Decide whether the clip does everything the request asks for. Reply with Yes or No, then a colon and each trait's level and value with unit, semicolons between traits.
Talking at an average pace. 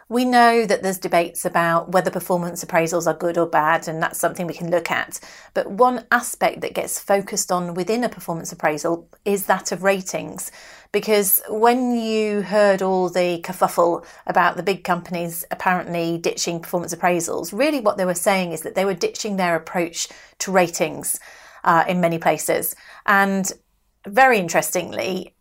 Yes: average, 170 wpm